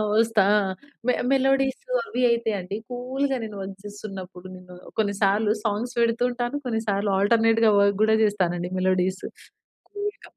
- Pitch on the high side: Yes, high, 220 Hz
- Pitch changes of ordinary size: Yes, average, 3.6 semitones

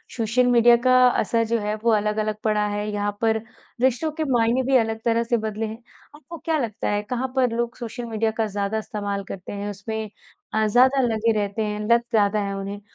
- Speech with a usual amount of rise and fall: No, narrow, 2.3 semitones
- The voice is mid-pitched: No, high, 220 Hz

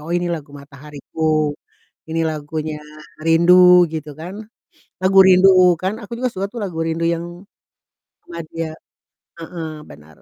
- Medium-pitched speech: Yes, medium, 165 Hz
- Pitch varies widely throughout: No, average, 2.8 semitones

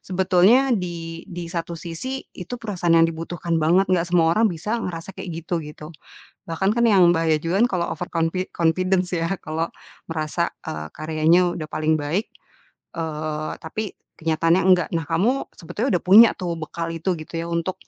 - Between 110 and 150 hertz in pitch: No, medium, 170 Hz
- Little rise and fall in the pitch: Yes, narrow, 2.3 semitones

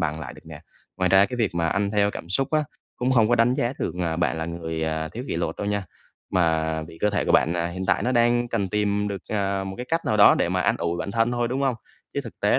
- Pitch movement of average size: No, wide, 5.9 semitones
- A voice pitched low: Yes, low, 100 Hz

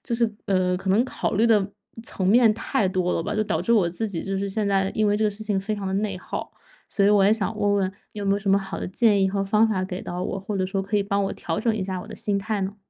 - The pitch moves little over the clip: Yes, narrow, 1.9 semitones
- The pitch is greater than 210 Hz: No, high, 200 Hz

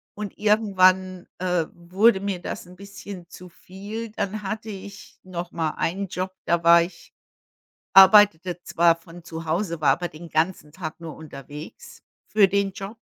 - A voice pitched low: No, medium, 185 Hz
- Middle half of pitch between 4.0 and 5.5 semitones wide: No, average, 2.9 semitones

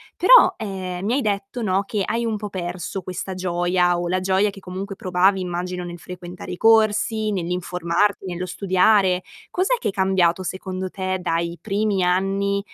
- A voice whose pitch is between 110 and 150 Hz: No, medium, 185 Hz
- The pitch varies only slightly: Yes, narrow, 2.1 semitones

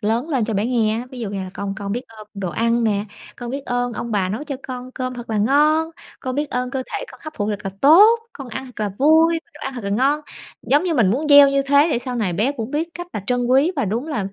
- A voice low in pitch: No, very high, 250 Hz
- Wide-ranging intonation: No, average, 4.8 semitones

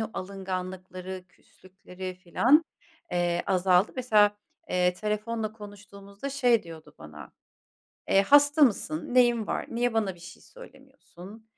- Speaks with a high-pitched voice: Yes, high, 200 Hz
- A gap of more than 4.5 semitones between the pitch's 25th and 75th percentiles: No, average, 4.1 semitones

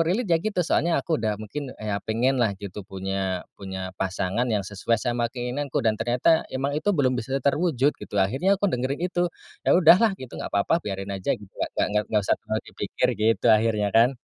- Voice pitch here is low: Yes, low, 120 Hz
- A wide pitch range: Yes, wide, 6.3 semitones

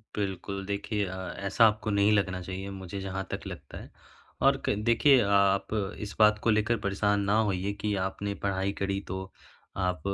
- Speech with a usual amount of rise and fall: No, narrow, 1.6 semitones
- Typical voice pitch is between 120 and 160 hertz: No, low, 100 Hz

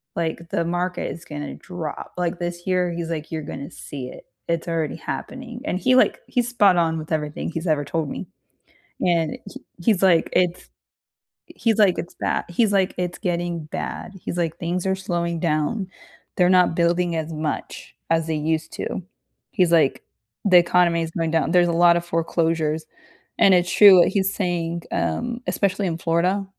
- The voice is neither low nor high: Yes, medium, 170 Hz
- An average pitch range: No, narrow, 1.9 semitones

